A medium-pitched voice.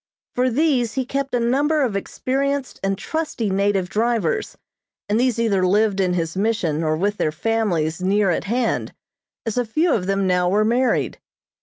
No: high, 220 Hz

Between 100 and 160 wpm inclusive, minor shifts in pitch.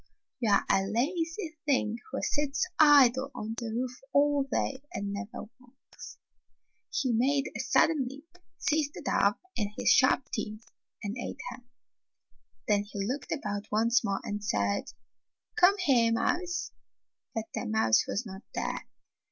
No: average, 150 wpm; wide, 5.5 semitones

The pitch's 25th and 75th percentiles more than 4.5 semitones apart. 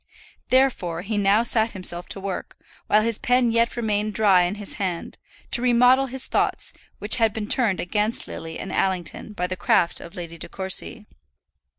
No: average, 4.0 semitones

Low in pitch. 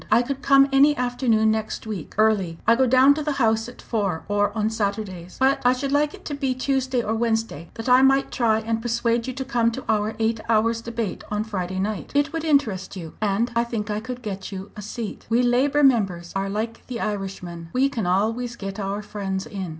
No: high, 225 Hz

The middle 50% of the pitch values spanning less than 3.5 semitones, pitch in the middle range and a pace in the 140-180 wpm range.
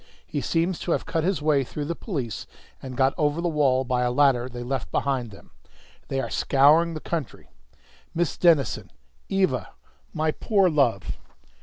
No: average, 4.3 semitones; medium, 145 Hz; average, 170 wpm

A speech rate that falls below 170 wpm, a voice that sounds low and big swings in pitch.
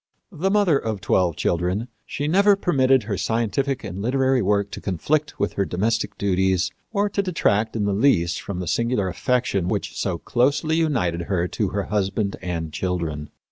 No: average, 175 wpm; low, 105 Hz; wide, 6.4 semitones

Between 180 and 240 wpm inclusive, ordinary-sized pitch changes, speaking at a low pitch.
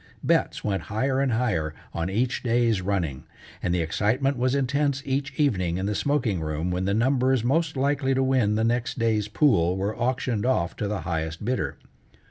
No: average, 185 wpm; wide, 5.8 semitones; low, 115 Hz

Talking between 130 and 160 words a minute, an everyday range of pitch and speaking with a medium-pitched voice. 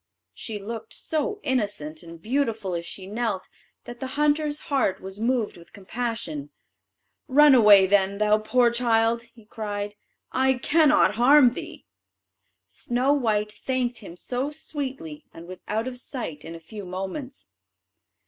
No: average, 145 wpm; average, 4.7 semitones; high, 225 Hz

